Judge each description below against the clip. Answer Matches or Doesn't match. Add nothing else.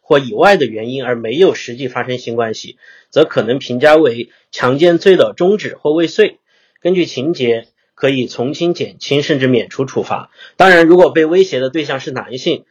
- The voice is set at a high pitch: Doesn't match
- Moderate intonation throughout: Doesn't match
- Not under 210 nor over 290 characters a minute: Matches